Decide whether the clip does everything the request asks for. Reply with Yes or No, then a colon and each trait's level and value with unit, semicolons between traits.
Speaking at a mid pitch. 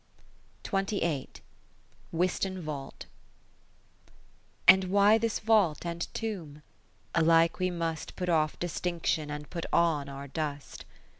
Yes: medium, 170 Hz